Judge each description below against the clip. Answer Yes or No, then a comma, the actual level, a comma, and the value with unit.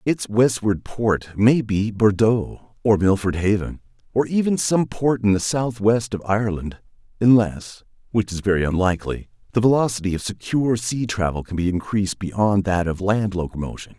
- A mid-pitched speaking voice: No, low, 105 Hz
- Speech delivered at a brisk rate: No, average, 155 wpm